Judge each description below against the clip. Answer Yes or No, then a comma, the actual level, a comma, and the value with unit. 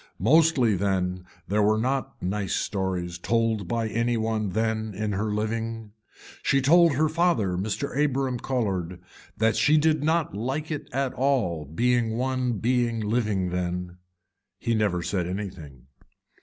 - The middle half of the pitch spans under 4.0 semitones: No, average, 5.2 semitones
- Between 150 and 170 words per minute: No, average, 140 wpm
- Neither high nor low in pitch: No, low, 110 Hz